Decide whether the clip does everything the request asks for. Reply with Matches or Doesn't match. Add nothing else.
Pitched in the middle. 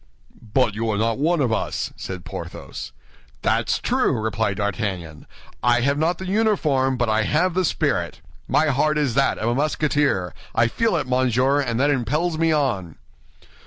Doesn't match